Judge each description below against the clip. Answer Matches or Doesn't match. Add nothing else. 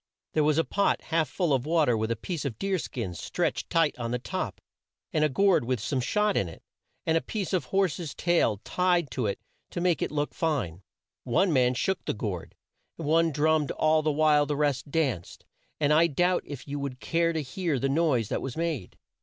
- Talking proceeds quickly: Matches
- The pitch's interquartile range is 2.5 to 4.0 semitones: Doesn't match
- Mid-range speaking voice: Matches